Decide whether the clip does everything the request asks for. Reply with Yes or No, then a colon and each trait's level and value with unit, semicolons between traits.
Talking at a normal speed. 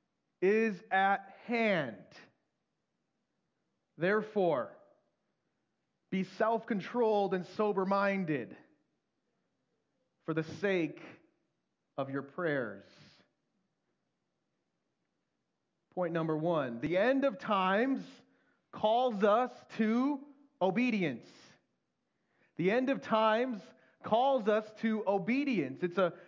No: slow, 85 wpm